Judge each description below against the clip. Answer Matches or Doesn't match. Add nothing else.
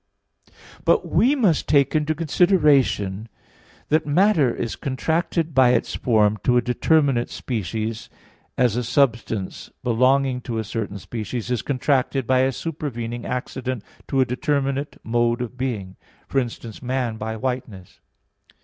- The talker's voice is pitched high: Doesn't match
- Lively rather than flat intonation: Doesn't match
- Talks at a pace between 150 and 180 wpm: Doesn't match